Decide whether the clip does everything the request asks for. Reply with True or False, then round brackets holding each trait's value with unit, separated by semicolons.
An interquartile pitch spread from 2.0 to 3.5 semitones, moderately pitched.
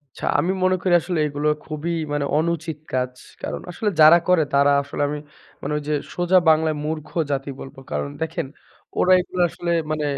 True (2.9 semitones; 155 Hz)